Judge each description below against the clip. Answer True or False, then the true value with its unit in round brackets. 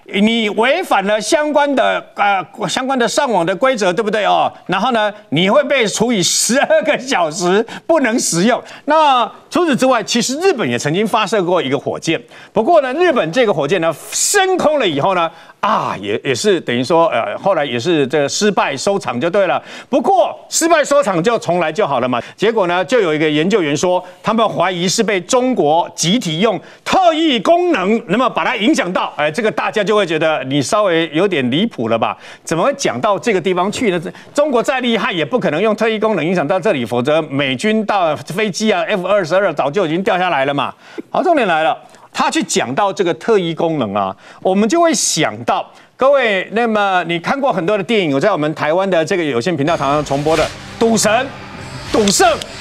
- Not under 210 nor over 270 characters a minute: False (300 characters per minute)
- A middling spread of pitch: False (6.5 semitones)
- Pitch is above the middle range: True (210 Hz)